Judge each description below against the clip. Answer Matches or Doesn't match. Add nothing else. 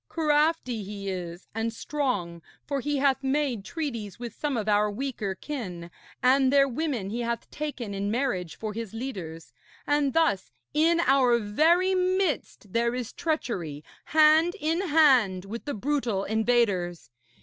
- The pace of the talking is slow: Doesn't match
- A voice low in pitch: Doesn't match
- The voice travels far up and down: Matches